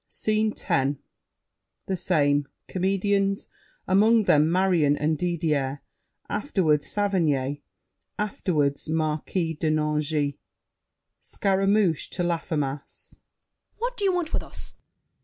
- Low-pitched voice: No, medium, 165 Hz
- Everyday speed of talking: No, slow, 100 wpm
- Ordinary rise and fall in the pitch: Yes, average, 4.9 semitones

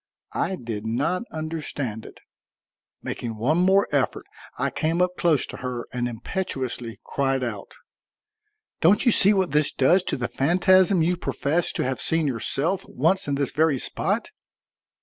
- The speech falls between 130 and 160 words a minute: Yes, average, 155 wpm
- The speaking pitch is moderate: Yes, medium, 150 Hz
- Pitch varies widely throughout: Yes, wide, 6.1 semitones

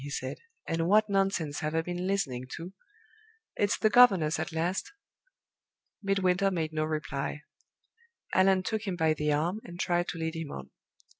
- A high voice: No, medium, 175 Hz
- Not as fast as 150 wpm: No, average, 165 wpm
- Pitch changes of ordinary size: Yes, average, 3.9 semitones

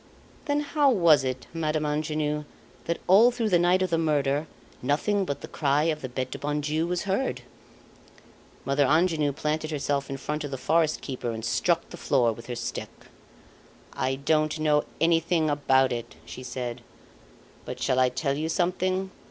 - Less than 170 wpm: No, average, 175 wpm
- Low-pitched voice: No, medium, 150 Hz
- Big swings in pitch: No, average, 3.7 semitones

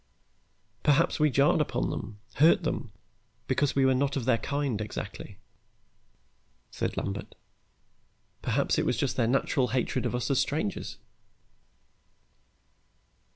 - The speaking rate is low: Yes, slow, 125 wpm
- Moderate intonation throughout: Yes, average, 3.2 semitones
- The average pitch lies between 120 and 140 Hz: Yes, low, 135 Hz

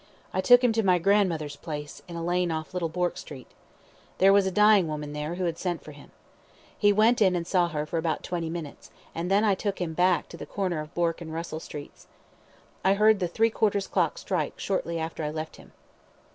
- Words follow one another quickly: Yes, fast, 220 wpm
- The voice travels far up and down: No, average, 3.5 semitones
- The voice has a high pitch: No, medium, 175 Hz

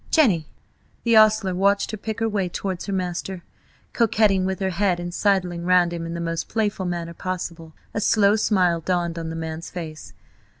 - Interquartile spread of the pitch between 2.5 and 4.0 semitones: Yes, average, 3.0 semitones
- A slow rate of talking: No, average, 185 wpm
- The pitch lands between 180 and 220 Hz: Yes, medium, 185 Hz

